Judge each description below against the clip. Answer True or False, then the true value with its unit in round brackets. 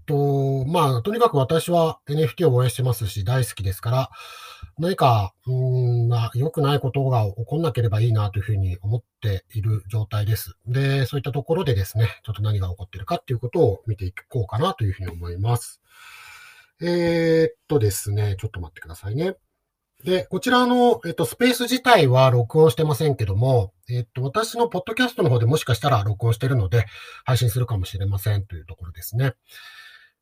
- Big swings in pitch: True (6.8 semitones)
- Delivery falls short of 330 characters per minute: False (405 characters per minute)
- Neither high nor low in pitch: False (125 Hz)